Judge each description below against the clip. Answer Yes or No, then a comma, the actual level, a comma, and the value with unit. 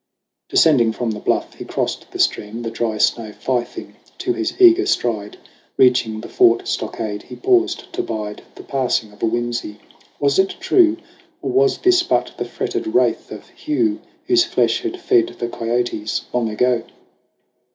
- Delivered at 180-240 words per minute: No, average, 165 wpm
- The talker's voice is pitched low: Yes, low, 125 Hz